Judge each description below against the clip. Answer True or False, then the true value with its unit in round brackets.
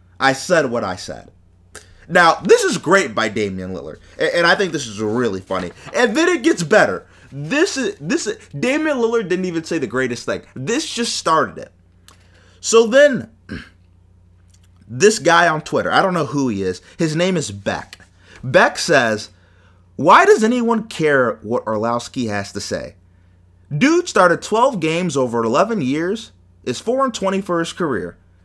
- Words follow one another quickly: False (170 wpm)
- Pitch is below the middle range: True (130 Hz)